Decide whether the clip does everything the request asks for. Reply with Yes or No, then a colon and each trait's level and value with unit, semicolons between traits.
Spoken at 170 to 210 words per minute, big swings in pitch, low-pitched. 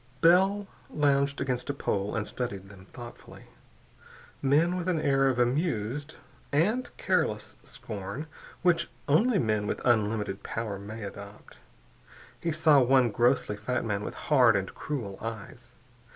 No: slow, 135 wpm; wide, 6.2 semitones; low, 125 Hz